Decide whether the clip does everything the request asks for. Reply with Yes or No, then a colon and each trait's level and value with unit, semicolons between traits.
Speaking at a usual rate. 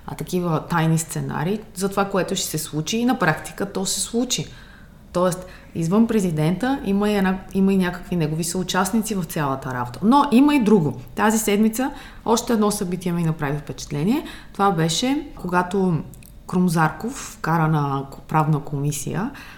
Yes: average, 155 wpm